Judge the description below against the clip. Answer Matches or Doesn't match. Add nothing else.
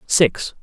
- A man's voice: Matches